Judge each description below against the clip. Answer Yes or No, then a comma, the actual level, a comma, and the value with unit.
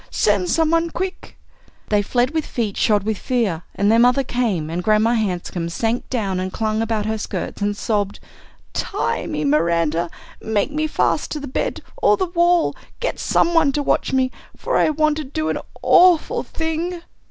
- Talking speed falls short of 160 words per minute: No, average, 185 wpm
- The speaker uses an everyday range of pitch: No, wide, 7.3 semitones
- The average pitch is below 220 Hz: No, high, 230 Hz